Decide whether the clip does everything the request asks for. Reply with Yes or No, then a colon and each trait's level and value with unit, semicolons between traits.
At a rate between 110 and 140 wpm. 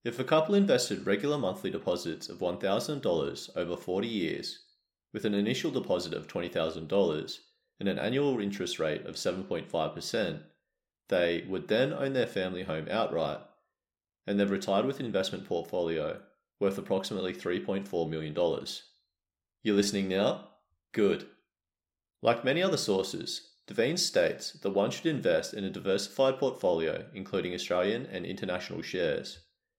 Yes: slow, 135 wpm